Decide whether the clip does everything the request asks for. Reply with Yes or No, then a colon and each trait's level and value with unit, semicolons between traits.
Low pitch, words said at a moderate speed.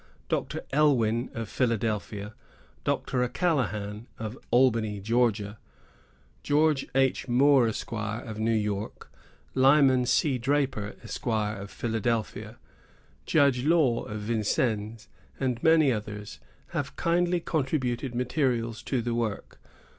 No: low, 120 Hz; slow, 105 wpm